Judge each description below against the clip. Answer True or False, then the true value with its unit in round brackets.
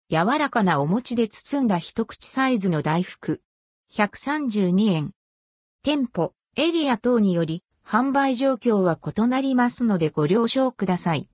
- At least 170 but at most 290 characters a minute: True (250 characters per minute)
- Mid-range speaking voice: False (225 Hz)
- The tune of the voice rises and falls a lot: True (6.4 semitones)